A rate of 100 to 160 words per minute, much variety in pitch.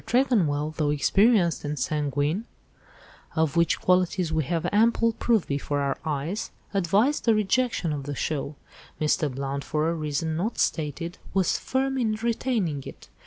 Yes: average, 140 wpm; wide, 6.5 semitones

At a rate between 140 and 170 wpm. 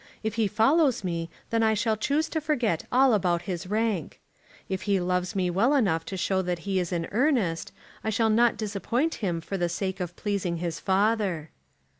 No: average, 195 wpm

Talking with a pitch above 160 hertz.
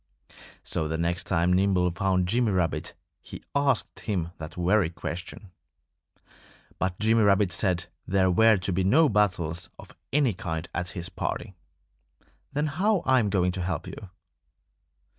No: very low, 95 Hz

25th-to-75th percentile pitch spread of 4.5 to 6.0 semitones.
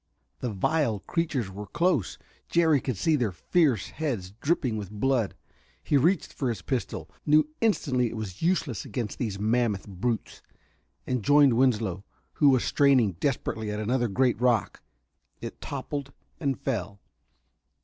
Yes: average, 5.3 semitones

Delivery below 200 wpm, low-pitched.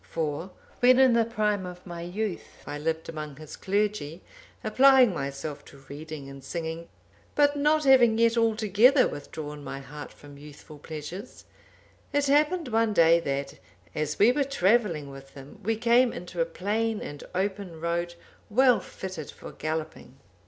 No: average, 155 wpm; medium, 180 Hz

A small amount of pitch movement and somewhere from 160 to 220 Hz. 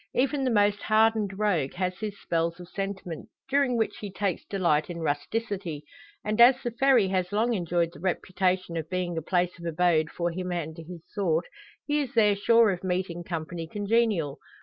No: average, 4.0 semitones; medium, 185 Hz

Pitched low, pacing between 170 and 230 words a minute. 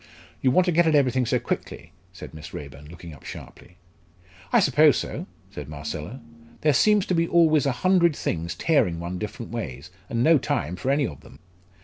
Yes: low, 125 Hz; average, 195 wpm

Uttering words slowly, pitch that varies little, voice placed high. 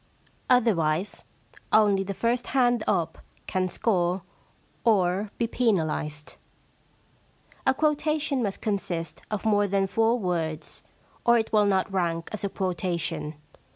No: slow, 130 wpm; average, 4.5 semitones; high, 200 Hz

